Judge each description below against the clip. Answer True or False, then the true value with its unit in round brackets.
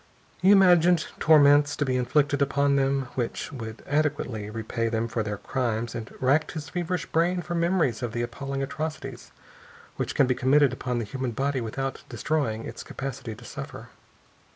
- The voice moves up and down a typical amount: True (4.1 semitones)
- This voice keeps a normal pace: True (170 wpm)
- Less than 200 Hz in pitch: True (135 Hz)